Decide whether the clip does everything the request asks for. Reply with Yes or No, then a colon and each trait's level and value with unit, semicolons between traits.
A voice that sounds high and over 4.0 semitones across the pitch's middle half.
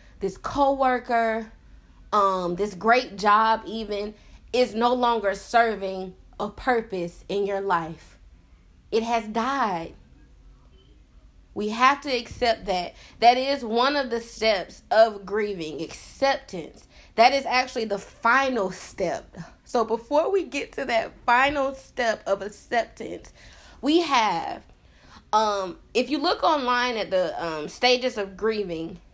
Yes: high, 225 Hz; average, 4.4 semitones